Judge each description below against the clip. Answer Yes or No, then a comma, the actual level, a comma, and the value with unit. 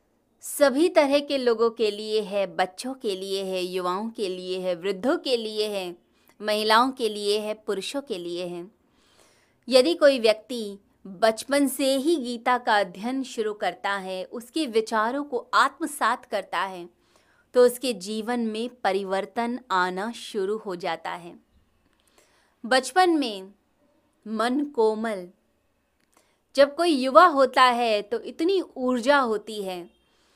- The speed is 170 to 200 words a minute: No, average, 135 wpm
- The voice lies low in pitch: No, high, 225 Hz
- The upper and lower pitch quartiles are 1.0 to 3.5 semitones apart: No, average, 4.9 semitones